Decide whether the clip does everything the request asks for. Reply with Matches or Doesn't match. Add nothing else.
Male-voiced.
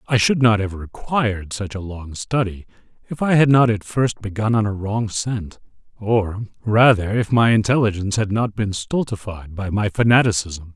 Matches